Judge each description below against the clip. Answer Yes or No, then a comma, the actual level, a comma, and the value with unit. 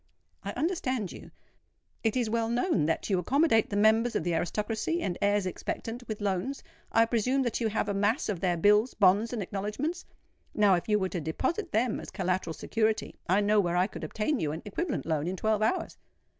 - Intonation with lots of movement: No, average, 3.9 semitones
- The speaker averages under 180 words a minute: No, fast, 205 wpm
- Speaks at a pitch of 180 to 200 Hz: No, high, 210 Hz